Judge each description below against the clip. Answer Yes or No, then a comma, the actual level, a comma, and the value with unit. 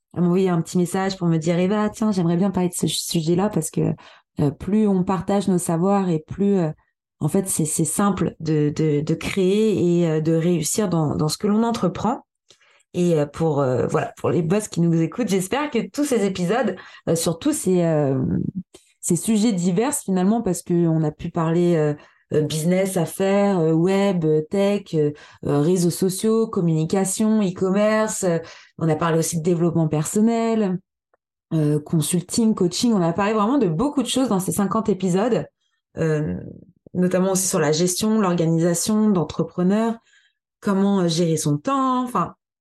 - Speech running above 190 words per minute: No, average, 180 wpm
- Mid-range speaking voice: Yes, medium, 180 Hz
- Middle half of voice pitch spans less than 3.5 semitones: No, average, 3.8 semitones